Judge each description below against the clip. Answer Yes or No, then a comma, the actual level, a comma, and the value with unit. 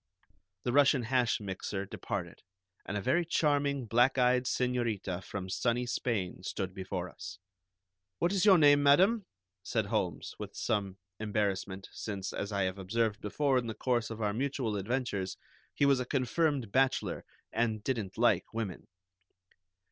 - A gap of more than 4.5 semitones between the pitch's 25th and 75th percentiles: Yes, average, 5.0 semitones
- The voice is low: Yes, low, 115 Hz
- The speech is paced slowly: No, average, 150 wpm